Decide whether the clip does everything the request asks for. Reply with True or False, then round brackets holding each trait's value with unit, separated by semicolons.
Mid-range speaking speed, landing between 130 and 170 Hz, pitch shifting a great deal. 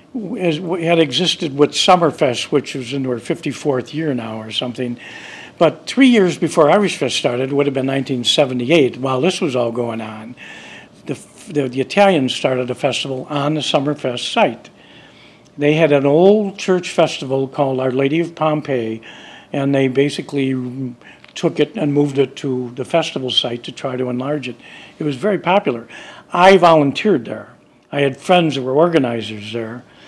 False (170 wpm; 140 Hz; 4.3 semitones)